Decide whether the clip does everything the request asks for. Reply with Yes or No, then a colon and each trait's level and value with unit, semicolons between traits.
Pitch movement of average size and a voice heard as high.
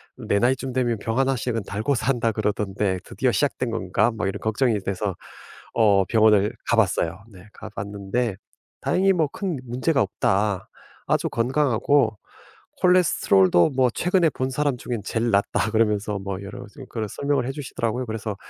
No: average, 4.3 semitones; low, 115 Hz